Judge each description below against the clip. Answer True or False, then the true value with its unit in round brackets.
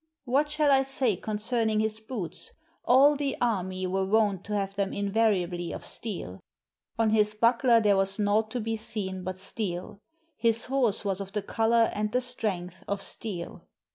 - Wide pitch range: False (3.1 semitones)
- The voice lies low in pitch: False (215 Hz)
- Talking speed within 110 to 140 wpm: False (170 wpm)